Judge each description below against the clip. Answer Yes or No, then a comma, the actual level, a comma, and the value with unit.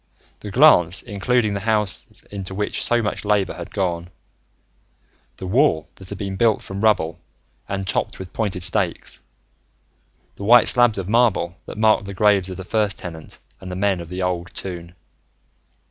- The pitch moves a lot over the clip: No, average, 2.8 semitones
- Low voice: Yes, very low, 95 Hz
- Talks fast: No, average, 170 wpm